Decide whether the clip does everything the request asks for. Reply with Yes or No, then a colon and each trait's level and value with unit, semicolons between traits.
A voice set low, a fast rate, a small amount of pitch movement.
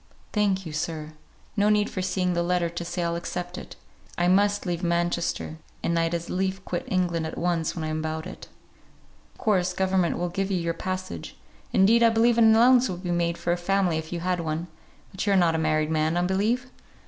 No: medium, 175 Hz; fast, 220 wpm; narrow, 2.3 semitones